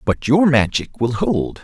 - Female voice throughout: No, male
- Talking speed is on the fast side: No, average, 185 wpm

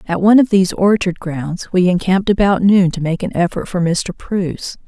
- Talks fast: Yes, fast, 210 wpm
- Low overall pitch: No, medium, 185 Hz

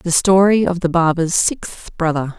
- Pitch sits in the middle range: Yes, medium, 175 Hz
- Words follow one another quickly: No, average, 175 wpm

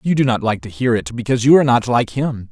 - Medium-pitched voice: No, low, 120 Hz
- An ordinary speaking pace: No, fast, 310 wpm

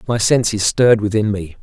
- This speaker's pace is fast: No, average, 185 wpm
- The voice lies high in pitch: No, low, 105 Hz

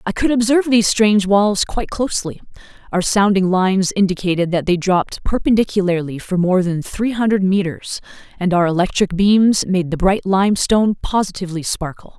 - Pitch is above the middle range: Yes, high, 195 Hz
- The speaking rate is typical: Yes, average, 160 wpm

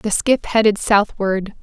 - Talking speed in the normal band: Yes, average, 150 wpm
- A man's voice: No, female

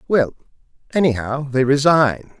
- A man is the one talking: Yes, male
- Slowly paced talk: Yes, slow, 100 wpm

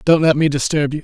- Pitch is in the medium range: Yes, medium, 150 Hz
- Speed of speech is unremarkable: No, fast, 290 wpm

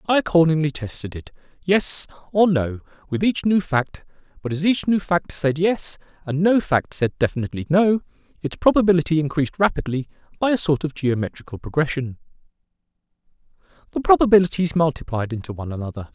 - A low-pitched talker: No, medium, 160 Hz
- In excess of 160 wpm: No, average, 150 wpm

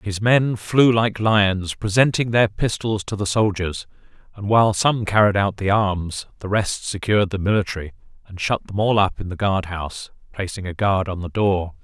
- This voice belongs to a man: Yes, male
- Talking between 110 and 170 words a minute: No, average, 195 wpm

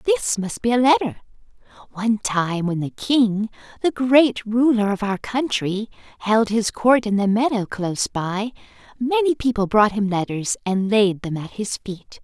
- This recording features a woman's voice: Yes, female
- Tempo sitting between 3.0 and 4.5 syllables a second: Yes, 4.4 syllables/s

